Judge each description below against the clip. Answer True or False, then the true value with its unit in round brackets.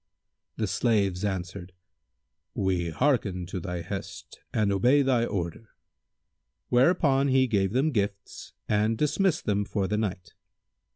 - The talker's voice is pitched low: True (105 Hz)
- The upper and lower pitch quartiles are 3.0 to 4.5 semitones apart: False (5.1 semitones)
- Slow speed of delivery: True (125 wpm)